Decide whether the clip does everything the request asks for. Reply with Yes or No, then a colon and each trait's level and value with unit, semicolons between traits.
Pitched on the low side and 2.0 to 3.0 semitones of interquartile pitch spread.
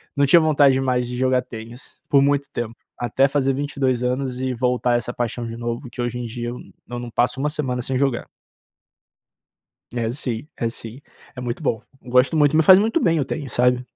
Yes: low, 125 Hz; narrow, 2.5 semitones